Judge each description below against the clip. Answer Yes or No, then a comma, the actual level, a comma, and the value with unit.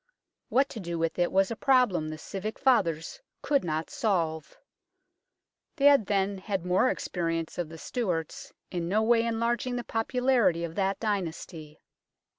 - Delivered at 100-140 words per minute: No, average, 155 wpm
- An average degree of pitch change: No, wide, 5.8 semitones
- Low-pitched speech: No, high, 195 Hz